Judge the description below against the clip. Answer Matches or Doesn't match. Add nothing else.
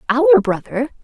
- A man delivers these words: Doesn't match